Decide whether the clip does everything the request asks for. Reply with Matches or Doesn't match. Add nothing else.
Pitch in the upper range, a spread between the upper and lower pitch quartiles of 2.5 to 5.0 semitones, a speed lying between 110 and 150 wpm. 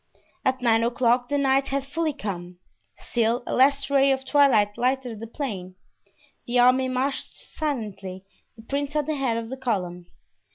Doesn't match